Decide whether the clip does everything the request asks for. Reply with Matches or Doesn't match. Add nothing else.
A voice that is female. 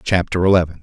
Doesn't match